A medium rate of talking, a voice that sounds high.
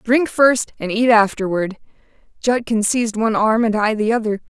Yes: average, 170 wpm; high, 225 Hz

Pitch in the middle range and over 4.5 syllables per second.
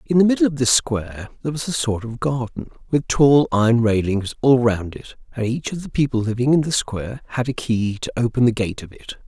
No: low, 125 Hz; 5.7 syllables/s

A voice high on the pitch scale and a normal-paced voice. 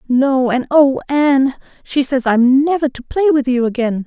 Yes: very high, 265 Hz; average, 190 wpm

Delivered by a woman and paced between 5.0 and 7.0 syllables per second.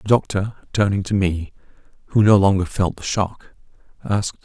No: male; 5.1 syllables/s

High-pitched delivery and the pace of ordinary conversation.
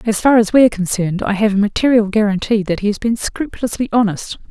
No: high, 215 Hz; fast, 225 wpm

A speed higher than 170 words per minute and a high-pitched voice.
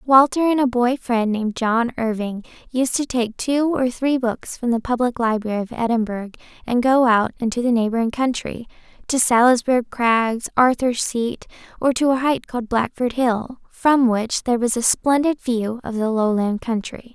Yes: average, 180 wpm; high, 240 Hz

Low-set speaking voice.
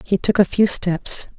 No: high, 195 Hz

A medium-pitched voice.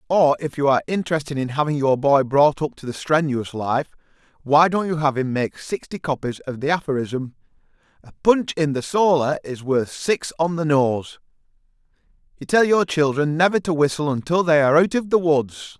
Yes: medium, 150 Hz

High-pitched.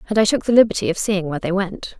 Yes: high, 195 Hz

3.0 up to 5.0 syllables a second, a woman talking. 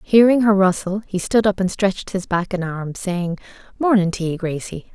Yes: 4.8 syllables/s; female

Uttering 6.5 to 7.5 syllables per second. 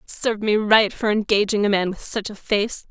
No: 5.1 syllables/s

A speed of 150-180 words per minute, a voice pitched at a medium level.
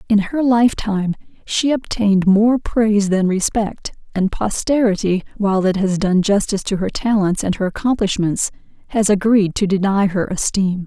No: average, 160 wpm; high, 205 Hz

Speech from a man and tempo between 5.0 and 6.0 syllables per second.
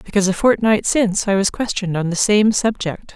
No: female; 5.9 syllables/s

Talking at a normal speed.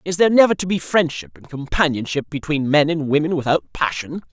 Yes: average, 195 wpm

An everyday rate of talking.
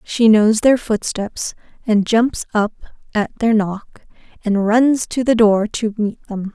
Yes: average, 165 wpm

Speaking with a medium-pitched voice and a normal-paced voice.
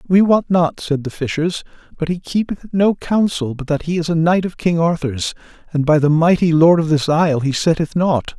No: medium, 165 Hz; fast, 230 wpm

